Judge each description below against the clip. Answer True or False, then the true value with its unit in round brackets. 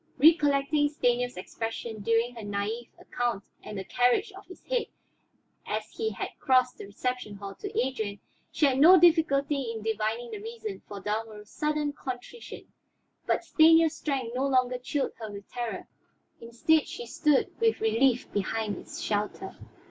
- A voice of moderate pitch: False (250 Hz)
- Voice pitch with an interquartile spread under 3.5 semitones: False (5.3 semitones)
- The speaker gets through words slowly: False (155 wpm)